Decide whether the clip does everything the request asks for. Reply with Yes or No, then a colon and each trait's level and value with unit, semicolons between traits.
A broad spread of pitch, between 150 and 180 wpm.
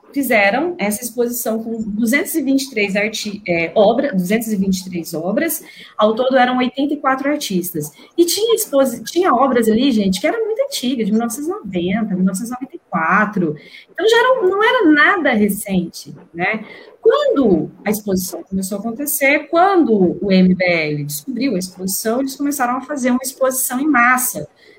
No: wide, 6.4 semitones; average, 140 wpm